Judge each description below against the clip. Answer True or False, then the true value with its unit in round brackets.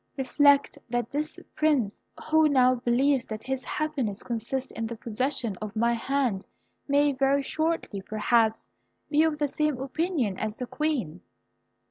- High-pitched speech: True (260 Hz)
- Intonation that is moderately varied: True (4.3 semitones)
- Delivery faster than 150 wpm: False (145 wpm)